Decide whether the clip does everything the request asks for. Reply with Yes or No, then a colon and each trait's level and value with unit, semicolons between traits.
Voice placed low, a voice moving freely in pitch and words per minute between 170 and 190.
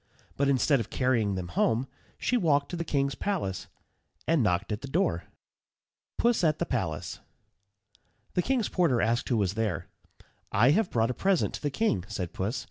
Yes: low, 130 Hz; wide, 7.6 semitones; average, 180 wpm